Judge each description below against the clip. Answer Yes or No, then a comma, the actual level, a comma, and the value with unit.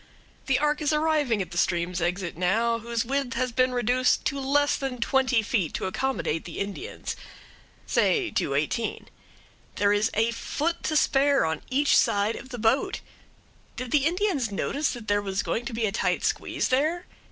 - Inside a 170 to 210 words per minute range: Yes, average, 180 wpm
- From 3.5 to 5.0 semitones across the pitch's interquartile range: No, wide, 5.5 semitones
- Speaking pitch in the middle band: No, high, 245 Hz